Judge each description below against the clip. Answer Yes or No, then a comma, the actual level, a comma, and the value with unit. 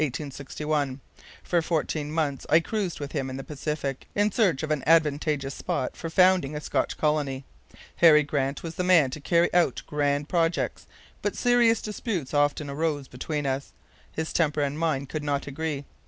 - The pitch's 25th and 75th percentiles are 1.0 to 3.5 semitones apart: Yes, average, 2.8 semitones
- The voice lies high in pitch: No, medium, 150 Hz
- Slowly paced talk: No, average, 170 wpm